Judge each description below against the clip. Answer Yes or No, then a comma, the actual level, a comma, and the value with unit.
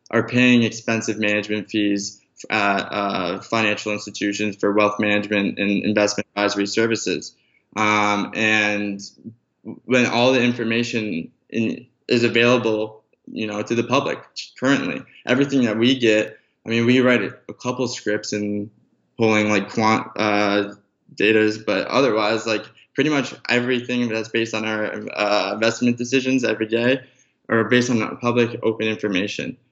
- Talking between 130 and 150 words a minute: Yes, average, 140 wpm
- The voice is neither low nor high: No, low, 110 Hz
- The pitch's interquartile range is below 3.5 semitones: Yes, narrow, 2.5 semitones